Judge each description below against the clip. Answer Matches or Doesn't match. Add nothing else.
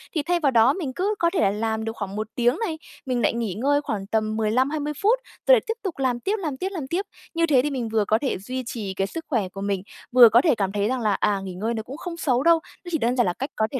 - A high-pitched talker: Matches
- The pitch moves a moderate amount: Doesn't match